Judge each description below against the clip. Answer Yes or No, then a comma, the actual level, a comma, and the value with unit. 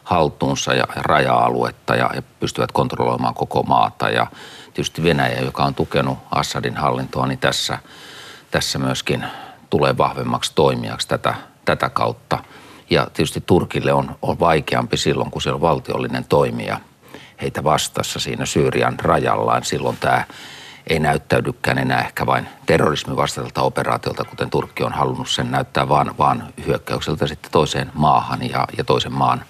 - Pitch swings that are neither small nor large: No, narrow, 1.9 semitones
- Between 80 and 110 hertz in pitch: No, very low, 65 Hz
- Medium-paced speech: Yes, average, 140 wpm